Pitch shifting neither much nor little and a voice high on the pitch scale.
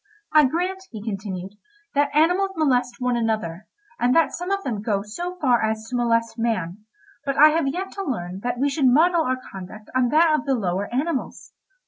No: wide, 6.0 semitones; very high, 250 Hz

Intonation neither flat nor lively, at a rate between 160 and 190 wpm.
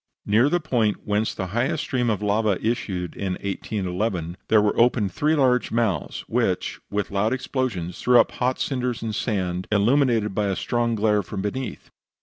Yes: average, 3.7 semitones; average, 170 wpm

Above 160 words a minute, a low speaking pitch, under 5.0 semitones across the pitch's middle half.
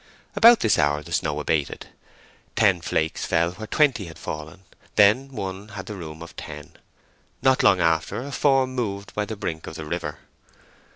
No: average, 175 wpm; very low, 95 Hz; wide, 5.6 semitones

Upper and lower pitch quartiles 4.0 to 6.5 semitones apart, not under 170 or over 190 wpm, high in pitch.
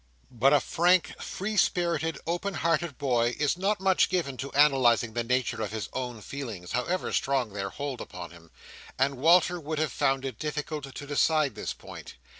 No: average, 5.3 semitones; average, 180 wpm; medium, 140 Hz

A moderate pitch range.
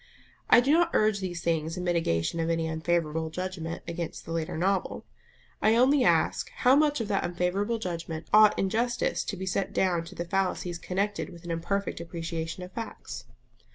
Yes: average, 3.7 semitones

